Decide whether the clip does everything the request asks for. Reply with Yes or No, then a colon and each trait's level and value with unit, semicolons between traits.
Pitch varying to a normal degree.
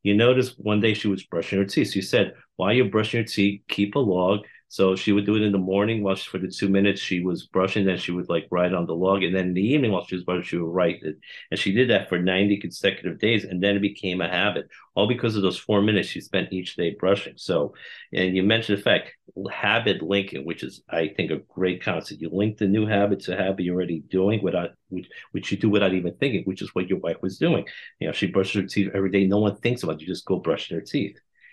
No: narrow, 1.9 semitones